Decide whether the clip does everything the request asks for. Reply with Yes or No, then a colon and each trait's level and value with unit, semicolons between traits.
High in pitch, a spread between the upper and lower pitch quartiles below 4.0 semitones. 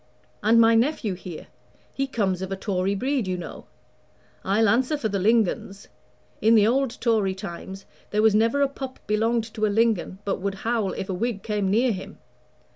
Yes: high, 215 Hz; average, 3.1 semitones